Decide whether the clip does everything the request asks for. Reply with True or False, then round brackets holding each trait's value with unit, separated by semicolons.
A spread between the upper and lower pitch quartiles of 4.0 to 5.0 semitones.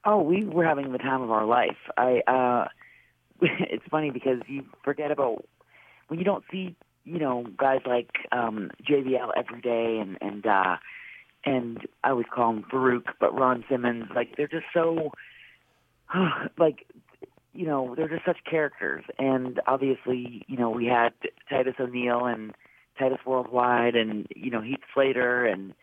False (3.0 semitones)